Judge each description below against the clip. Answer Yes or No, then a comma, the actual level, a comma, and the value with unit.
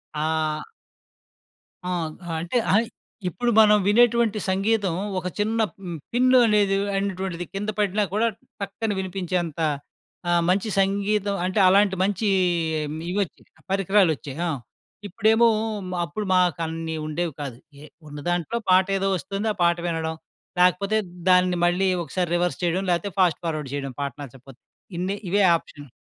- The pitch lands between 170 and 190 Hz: Yes, medium, 185 Hz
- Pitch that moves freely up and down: No, average, 3.3 semitones